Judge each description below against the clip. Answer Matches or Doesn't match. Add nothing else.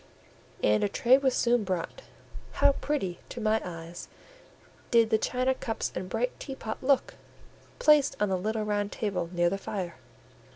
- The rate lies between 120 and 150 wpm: Doesn't match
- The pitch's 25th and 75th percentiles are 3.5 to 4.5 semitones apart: Doesn't match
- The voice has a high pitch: Matches